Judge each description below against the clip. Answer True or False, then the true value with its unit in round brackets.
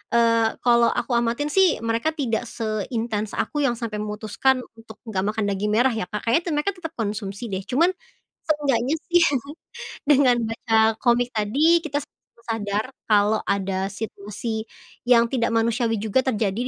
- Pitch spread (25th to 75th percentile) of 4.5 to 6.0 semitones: False (3.3 semitones)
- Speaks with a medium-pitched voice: False (230 Hz)